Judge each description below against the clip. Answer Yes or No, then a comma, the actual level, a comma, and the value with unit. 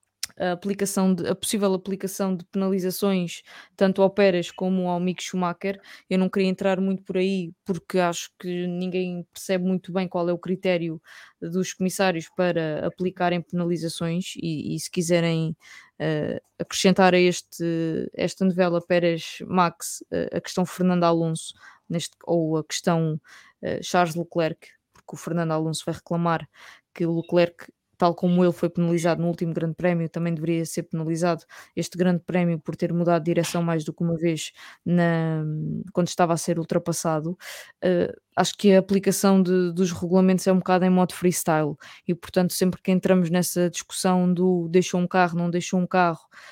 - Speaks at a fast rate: No, average, 170 wpm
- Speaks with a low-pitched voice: No, medium, 180 Hz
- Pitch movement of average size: No, narrow, 1.7 semitones